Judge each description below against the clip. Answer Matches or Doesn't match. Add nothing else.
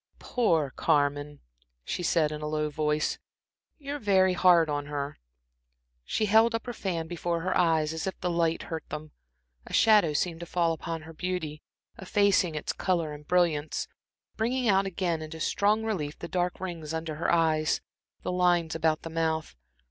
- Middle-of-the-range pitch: Matches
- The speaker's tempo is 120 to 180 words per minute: Matches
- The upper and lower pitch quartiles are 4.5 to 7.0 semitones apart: Doesn't match